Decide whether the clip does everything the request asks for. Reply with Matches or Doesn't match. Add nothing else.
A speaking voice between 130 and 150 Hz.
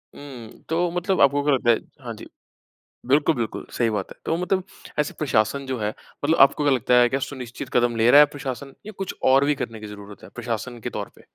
Matches